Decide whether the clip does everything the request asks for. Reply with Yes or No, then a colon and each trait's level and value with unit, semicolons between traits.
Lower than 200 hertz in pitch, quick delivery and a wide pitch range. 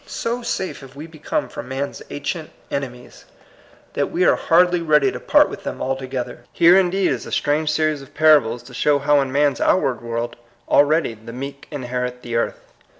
No: medium, 140 Hz; fast, 210 wpm; average, 3.9 semitones